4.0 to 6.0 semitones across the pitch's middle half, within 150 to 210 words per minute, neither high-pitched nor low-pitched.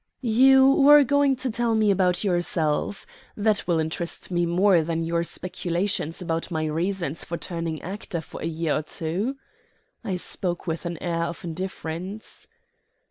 No: average, 3.5 semitones; average, 160 wpm; medium, 175 Hz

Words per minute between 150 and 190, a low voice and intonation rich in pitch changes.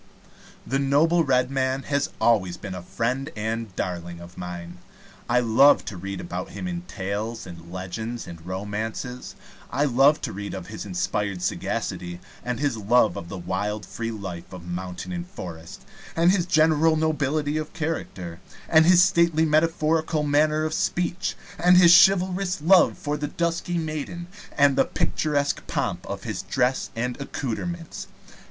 Yes: average, 160 wpm; low, 130 Hz; wide, 8.3 semitones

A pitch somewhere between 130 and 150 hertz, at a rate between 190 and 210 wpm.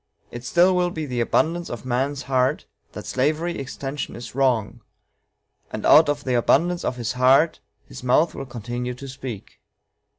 No: low, 135 Hz; average, 165 wpm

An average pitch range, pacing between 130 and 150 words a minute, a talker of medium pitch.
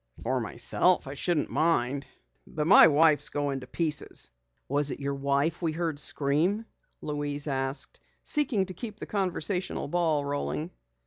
Yes: average, 3.7 semitones; average, 145 wpm; medium, 150 Hz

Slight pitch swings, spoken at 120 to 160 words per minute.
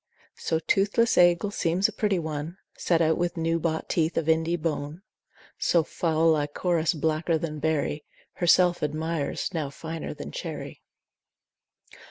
Yes: narrow, 1.8 semitones; average, 140 wpm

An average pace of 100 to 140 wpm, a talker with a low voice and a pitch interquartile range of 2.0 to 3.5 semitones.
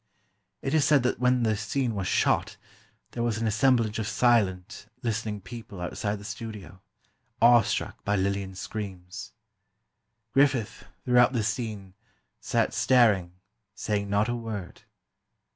Yes: slow, 135 wpm; low, 110 Hz; average, 3.1 semitones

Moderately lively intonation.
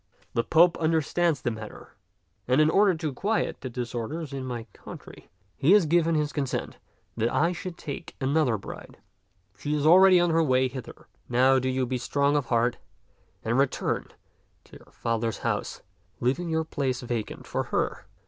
Yes: average, 4.6 semitones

